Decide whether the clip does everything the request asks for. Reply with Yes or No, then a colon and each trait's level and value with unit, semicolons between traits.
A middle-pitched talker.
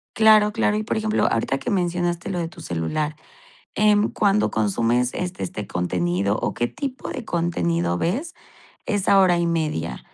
Yes: medium, 170 Hz